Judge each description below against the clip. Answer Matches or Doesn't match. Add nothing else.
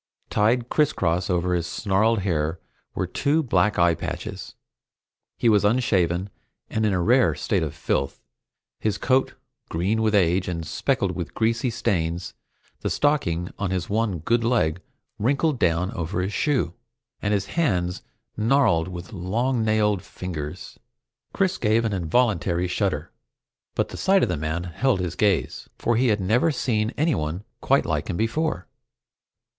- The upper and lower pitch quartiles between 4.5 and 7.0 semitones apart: Matches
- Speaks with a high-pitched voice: Doesn't match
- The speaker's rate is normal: Matches